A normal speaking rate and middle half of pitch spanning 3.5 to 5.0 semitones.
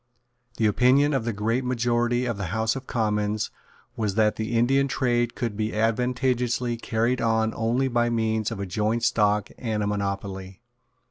No: average, 170 wpm; narrow, 2.4 semitones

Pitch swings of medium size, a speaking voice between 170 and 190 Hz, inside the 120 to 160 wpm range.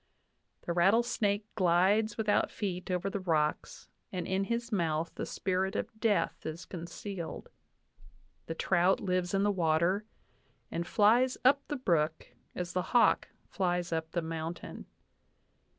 Yes: average, 3.4 semitones; medium, 185 Hz; average, 140 wpm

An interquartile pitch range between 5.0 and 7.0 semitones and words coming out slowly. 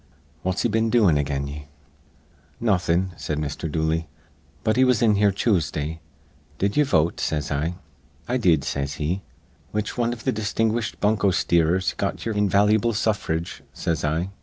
No: wide, 5.5 semitones; average, 160 wpm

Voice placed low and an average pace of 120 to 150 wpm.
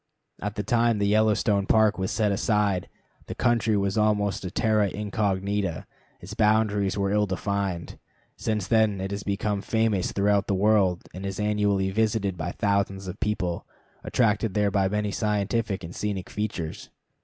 No: low, 100 Hz; average, 160 wpm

